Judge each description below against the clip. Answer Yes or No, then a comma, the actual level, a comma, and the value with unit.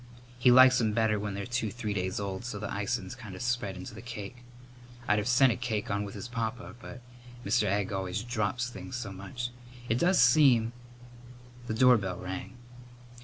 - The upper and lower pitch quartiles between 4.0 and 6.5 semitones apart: No, average, 3.4 semitones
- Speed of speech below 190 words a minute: No, average, 195 wpm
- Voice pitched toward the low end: Yes, low, 115 Hz